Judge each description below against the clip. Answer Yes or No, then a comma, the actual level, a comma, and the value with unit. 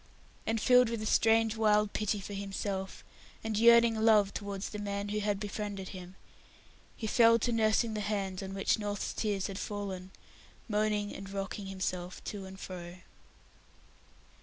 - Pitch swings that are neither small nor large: No, narrow, 1.9 semitones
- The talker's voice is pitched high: Yes, high, 205 Hz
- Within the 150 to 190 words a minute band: Yes, average, 155 wpm